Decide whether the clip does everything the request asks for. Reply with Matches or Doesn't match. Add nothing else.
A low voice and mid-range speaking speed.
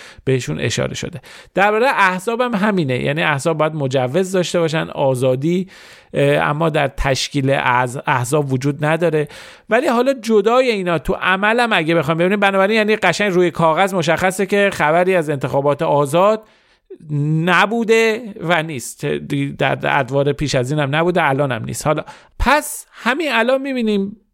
Doesn't match